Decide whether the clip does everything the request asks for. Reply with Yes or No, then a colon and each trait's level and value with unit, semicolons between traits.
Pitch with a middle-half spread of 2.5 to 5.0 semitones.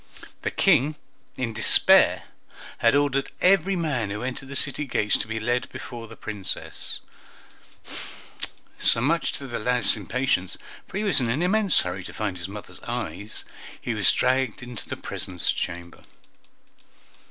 Yes: average, 4.7 semitones